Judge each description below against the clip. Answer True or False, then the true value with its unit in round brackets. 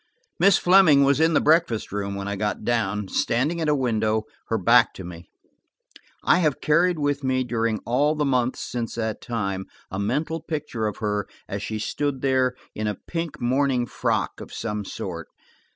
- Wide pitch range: True (5.8 semitones)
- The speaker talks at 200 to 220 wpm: False (185 wpm)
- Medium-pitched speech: False (120 Hz)